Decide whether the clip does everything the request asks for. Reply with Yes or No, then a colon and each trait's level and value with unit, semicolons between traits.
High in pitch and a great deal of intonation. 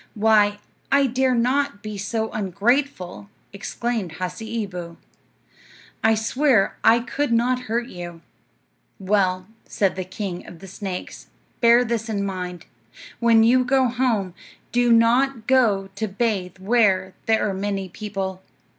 No: high, 215 Hz; average, 3.8 semitones